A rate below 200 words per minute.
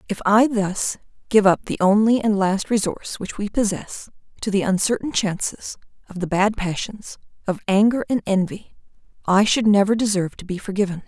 Yes: average, 175 wpm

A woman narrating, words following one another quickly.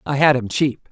Yes: female; fast, 260 wpm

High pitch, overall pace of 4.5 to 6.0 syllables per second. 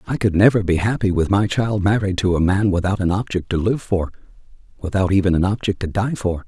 No: very low, 95 Hz; 5.9 syllables/s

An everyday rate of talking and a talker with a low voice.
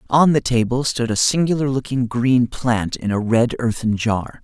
Yes: average, 190 wpm; low, 120 Hz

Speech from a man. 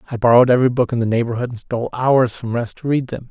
Yes: male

